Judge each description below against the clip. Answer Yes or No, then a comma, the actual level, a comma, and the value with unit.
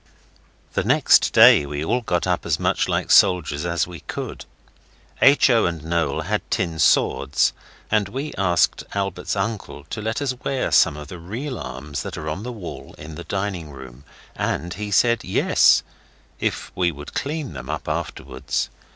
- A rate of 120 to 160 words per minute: No, average, 175 wpm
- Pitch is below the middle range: Yes, very low, 90 Hz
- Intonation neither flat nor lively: No, wide, 6.0 semitones